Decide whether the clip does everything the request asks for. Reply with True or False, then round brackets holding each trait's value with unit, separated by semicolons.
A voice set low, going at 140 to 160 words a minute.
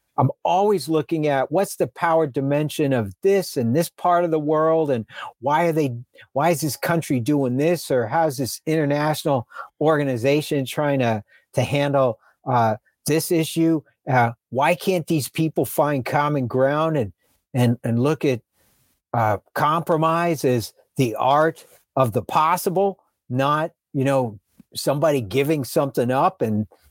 False (145 Hz; 150 wpm)